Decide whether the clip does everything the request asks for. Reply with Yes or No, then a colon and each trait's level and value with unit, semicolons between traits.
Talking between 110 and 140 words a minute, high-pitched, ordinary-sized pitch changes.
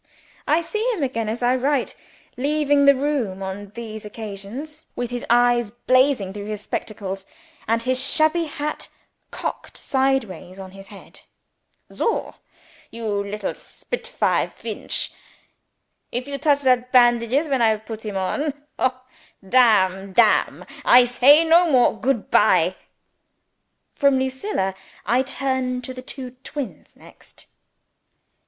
Yes: slow, 135 wpm; very high, 250 Hz; average, 4.6 semitones